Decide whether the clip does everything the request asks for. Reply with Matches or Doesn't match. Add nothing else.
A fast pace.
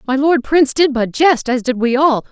Matches